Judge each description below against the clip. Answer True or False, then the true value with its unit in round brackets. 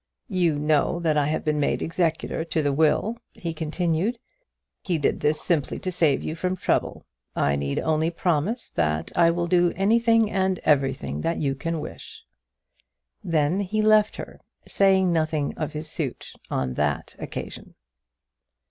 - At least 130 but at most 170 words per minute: True (155 wpm)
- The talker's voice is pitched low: False (160 Hz)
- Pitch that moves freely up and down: False (3.7 semitones)